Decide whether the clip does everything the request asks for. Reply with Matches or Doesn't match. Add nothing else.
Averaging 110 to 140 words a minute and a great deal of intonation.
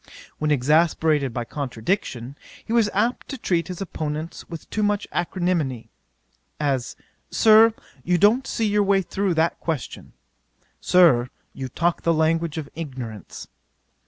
Matches